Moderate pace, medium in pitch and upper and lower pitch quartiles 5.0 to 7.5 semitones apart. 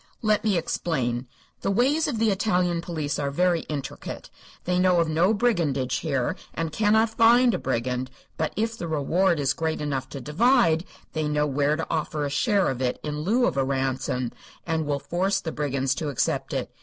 Yes: average, 195 wpm; medium, 160 Hz; wide, 5.6 semitones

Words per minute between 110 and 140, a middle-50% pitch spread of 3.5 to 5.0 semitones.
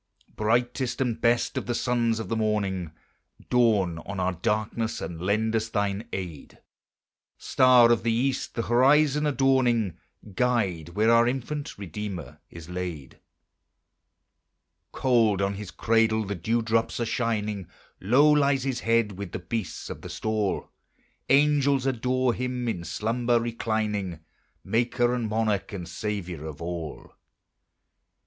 Yes: slow, 135 wpm; average, 3.8 semitones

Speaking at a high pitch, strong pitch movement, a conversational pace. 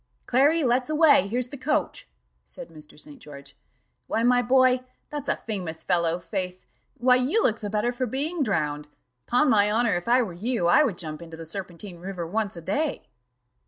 Yes: high, 215 Hz; wide, 6.7 semitones; average, 185 wpm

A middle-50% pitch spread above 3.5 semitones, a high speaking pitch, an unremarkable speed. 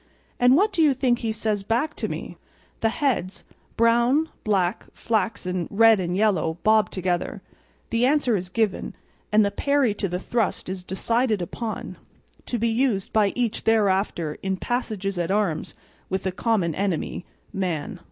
Yes: average, 3.9 semitones; high, 215 Hz; average, 160 wpm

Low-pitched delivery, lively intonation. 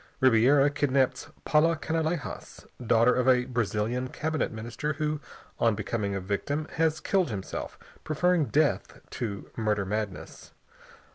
Yes: low, 130 Hz; wide, 5.8 semitones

